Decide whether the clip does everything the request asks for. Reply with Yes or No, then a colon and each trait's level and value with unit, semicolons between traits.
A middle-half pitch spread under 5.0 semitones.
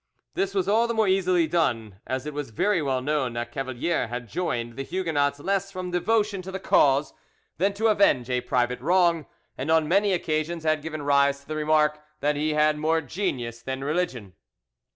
No: wide, 5.4 semitones